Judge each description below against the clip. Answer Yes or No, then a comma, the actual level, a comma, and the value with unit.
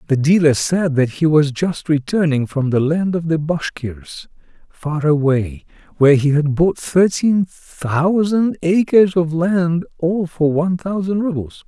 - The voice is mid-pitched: Yes, medium, 160 Hz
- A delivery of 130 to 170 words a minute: Yes, average, 155 wpm